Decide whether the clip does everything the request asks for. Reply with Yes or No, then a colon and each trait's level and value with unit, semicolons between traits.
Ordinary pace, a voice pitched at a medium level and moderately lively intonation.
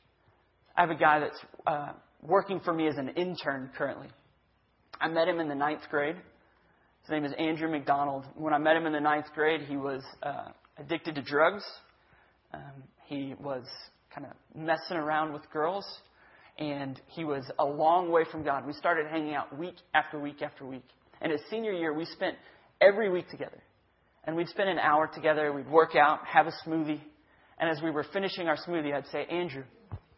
No: average, 190 wpm; medium, 155 Hz; narrow, 2.3 semitones